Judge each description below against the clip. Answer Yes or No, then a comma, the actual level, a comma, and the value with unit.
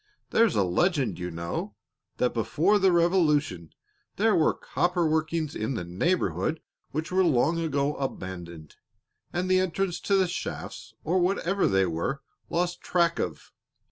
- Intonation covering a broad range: Yes, wide, 7.6 semitones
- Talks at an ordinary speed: Yes, average, 145 wpm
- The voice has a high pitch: No, medium, 160 Hz